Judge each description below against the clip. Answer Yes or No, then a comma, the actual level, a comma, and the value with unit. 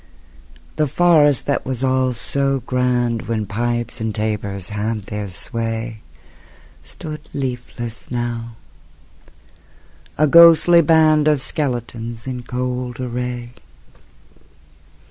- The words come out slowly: Yes, slow, 100 wpm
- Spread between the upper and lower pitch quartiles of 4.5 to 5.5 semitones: No, average, 3.1 semitones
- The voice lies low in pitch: Yes, low, 125 Hz